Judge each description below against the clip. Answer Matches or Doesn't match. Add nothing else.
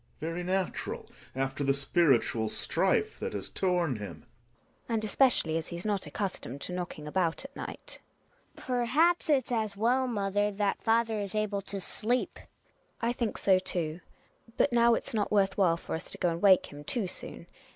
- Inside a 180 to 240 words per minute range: Matches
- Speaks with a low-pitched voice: Doesn't match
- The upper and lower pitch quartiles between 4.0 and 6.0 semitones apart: Matches